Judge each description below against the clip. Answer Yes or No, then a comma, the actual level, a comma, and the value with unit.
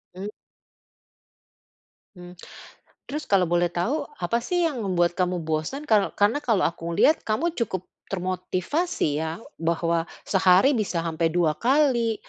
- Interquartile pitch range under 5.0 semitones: No, wide, 5.6 semitones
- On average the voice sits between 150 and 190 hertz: Yes, medium, 185 Hz